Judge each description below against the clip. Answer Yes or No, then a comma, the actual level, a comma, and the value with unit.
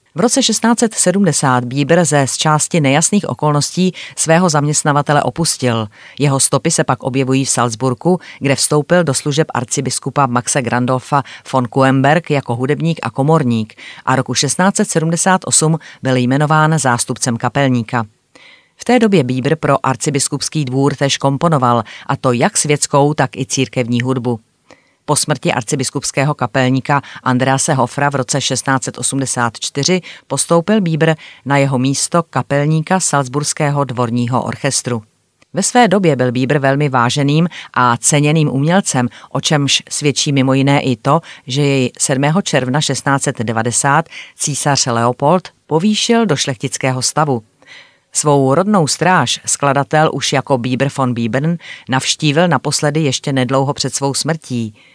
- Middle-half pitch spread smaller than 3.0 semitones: No, average, 3.3 semitones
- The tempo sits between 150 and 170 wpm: No, average, 130 wpm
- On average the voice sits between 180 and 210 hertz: No, medium, 140 Hz